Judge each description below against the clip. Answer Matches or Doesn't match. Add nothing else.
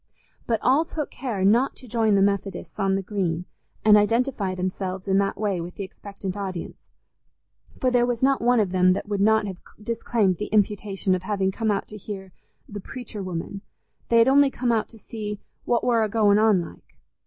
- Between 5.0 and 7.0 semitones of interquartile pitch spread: Doesn't match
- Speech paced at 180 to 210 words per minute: Matches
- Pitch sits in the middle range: Doesn't match